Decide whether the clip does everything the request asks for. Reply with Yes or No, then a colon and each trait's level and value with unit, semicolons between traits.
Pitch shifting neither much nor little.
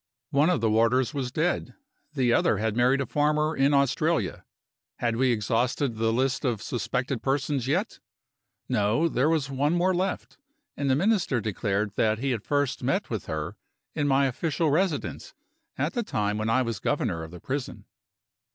Yes: average, 4.6 semitones